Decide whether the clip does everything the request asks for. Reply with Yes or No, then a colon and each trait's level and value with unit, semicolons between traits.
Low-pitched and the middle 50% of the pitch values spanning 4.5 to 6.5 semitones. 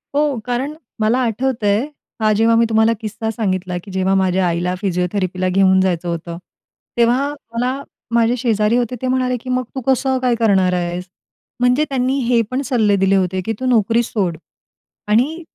No: high, 225 Hz; average, 4.9 semitones